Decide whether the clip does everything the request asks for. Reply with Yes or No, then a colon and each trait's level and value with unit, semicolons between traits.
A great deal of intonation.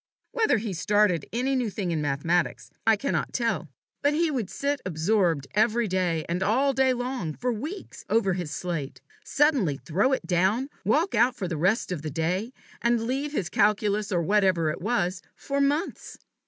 Yes: wide, 6.4 semitones